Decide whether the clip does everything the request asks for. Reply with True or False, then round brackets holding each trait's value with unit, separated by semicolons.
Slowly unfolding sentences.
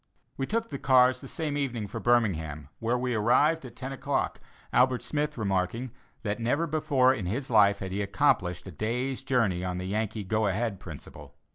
False (185 wpm)